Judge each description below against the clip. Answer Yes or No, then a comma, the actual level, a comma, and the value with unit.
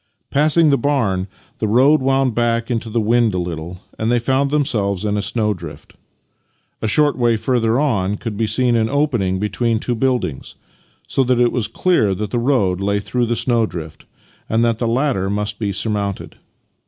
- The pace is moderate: Yes, average, 180 wpm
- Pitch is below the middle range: Yes, low, 115 Hz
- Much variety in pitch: No, average, 3.8 semitones